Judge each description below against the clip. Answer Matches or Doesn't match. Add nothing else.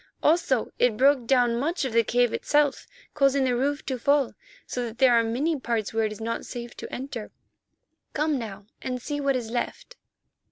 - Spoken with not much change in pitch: Doesn't match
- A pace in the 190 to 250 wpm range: Matches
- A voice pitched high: Matches